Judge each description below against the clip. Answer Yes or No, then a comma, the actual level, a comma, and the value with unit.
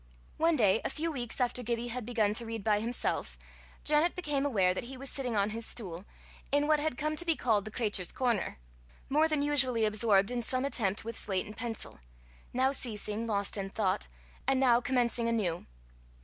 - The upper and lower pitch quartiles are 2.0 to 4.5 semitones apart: Yes, average, 4.1 semitones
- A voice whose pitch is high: Yes, high, 235 Hz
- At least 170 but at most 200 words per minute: Yes, average, 195 wpm